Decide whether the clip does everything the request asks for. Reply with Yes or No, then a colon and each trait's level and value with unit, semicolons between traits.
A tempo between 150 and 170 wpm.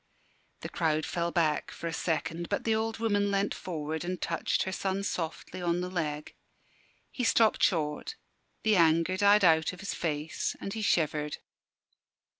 Yes: average, 165 wpm